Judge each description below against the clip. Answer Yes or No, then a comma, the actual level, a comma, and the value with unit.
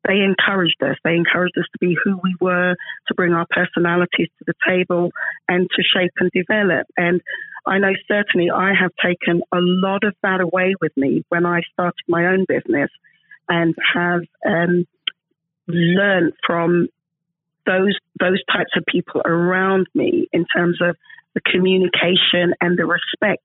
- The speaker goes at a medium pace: Yes, average, 160 wpm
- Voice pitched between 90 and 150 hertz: No, medium, 180 Hz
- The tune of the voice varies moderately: No, narrow, 1.6 semitones